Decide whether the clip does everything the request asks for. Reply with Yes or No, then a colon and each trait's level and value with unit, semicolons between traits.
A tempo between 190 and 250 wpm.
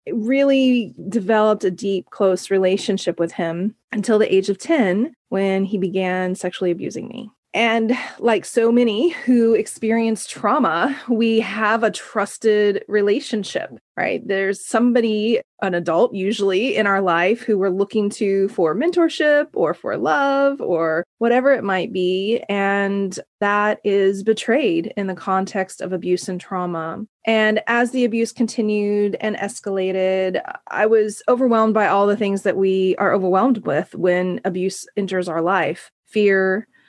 No: average, 150 wpm